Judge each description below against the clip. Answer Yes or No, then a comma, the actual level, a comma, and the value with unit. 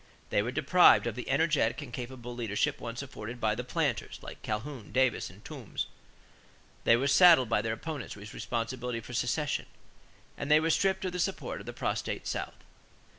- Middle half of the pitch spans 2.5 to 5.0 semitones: Yes, average, 4.4 semitones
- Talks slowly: No, average, 180 wpm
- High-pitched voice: No, low, 125 Hz